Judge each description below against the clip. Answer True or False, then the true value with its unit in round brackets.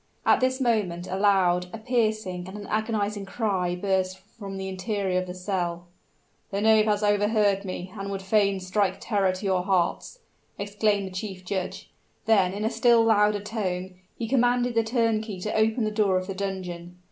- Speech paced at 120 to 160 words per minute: False (180 wpm)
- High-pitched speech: True (200 Hz)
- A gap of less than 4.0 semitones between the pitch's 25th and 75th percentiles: True (2.6 semitones)